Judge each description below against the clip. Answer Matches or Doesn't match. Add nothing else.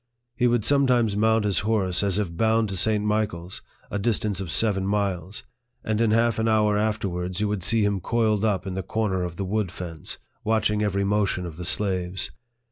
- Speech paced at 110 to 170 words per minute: Doesn't match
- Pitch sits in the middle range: Doesn't match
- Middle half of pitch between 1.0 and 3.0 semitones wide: Matches